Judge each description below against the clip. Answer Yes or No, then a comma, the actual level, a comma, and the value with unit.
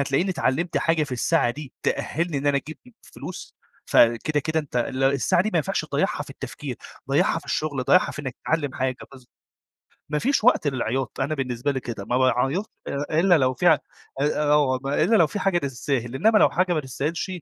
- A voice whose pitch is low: No, medium, 145 Hz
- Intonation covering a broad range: No, average, 4.0 semitones